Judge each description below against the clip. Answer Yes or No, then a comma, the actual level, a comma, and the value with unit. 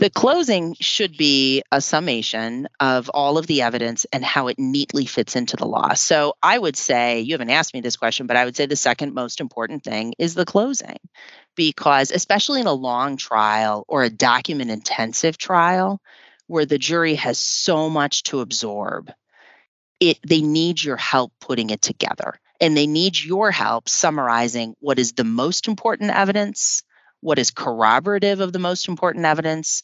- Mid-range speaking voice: Yes, medium, 150 Hz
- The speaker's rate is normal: Yes, average, 175 wpm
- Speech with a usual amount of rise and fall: No, wide, 6.5 semitones